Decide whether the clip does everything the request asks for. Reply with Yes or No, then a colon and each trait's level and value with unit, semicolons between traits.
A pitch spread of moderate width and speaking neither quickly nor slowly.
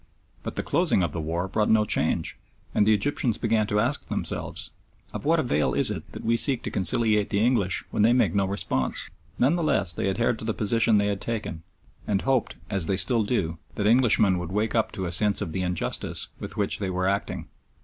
No: average, 3.4 semitones; fast, 220 wpm